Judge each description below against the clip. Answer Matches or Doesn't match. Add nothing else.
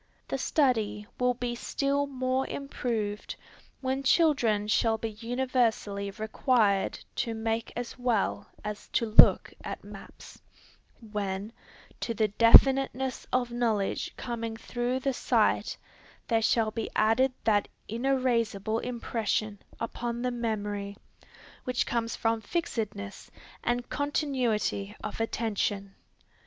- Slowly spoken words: Matches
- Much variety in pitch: Doesn't match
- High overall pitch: Matches